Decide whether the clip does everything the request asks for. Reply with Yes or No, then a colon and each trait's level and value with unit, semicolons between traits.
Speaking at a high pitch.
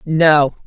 No: medium, 155 Hz